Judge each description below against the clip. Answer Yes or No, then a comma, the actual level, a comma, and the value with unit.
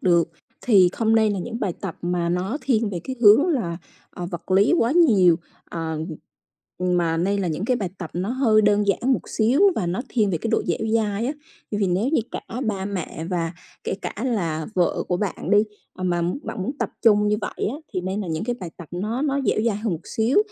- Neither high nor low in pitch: No, high, 200 Hz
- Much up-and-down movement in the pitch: No, average, 4.3 semitones